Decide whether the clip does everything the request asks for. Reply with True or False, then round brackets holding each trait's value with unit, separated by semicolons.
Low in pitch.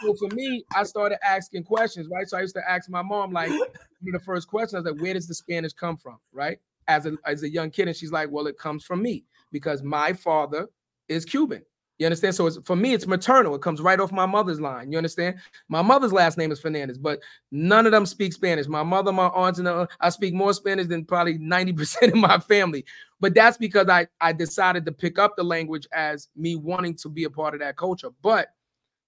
False (180 Hz)